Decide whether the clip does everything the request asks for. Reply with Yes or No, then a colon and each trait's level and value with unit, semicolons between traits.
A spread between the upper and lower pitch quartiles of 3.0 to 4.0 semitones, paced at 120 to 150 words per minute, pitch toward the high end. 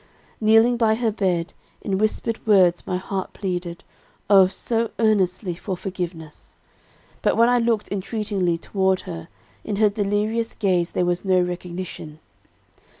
Yes: average, 3.3 semitones; average, 140 wpm; high, 195 Hz